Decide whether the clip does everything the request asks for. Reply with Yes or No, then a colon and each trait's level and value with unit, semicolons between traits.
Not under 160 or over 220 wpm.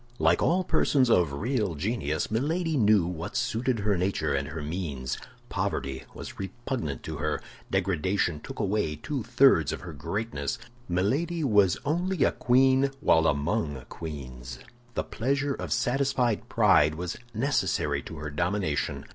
No: average, 145 wpm